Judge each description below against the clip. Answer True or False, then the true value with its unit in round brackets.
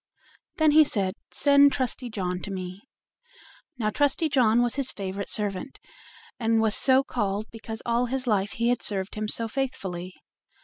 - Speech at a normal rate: True (165 wpm)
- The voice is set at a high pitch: True (225 Hz)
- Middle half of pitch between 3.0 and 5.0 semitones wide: True (4.6 semitones)